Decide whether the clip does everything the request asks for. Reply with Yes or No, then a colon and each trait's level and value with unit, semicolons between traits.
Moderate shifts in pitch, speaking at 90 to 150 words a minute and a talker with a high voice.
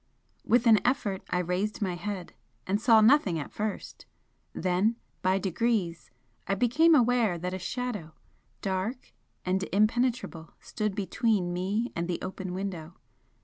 Yes: average, 4.1 semitones; average, 140 wpm; high, 195 Hz